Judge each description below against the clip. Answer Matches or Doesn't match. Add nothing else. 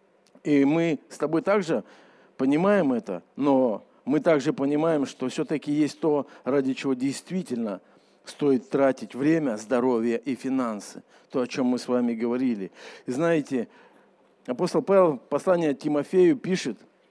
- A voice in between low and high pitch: Matches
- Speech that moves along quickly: Doesn't match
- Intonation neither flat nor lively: Matches